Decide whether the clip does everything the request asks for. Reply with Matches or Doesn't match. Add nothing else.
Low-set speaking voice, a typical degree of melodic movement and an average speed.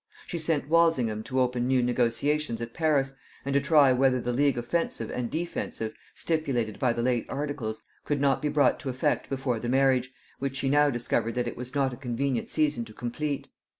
Matches